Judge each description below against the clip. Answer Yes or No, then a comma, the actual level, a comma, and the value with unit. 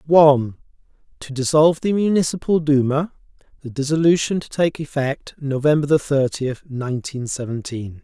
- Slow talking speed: Yes, slow, 110 wpm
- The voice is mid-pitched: Yes, medium, 145 Hz